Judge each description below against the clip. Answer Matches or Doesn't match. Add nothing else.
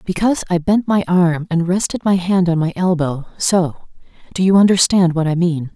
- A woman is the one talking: Matches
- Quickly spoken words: Doesn't match